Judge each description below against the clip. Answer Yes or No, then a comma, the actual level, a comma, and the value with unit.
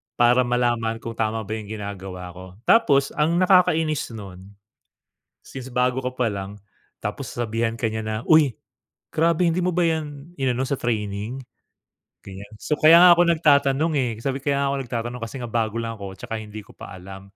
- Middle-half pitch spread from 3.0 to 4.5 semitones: No, average, 4.9 semitones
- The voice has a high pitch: No, low, 120 Hz